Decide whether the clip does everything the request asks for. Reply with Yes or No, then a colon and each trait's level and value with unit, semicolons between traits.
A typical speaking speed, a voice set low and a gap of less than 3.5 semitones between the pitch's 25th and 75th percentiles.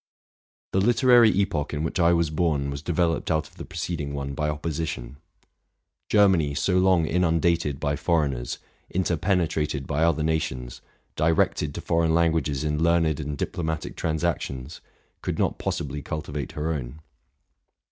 Yes: average, 145 wpm; very low, 80 Hz; narrow, 2.6 semitones